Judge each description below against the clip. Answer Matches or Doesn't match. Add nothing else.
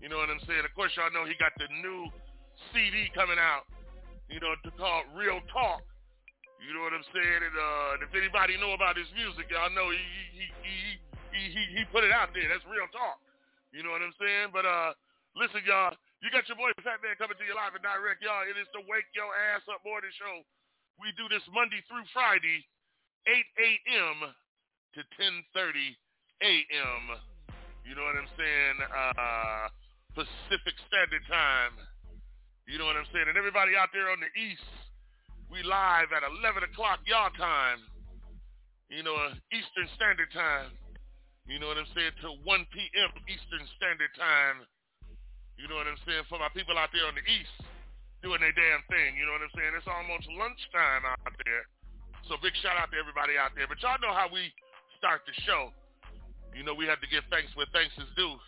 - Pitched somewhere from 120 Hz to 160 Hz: Doesn't match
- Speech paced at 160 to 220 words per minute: Matches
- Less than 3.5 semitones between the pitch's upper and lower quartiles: Doesn't match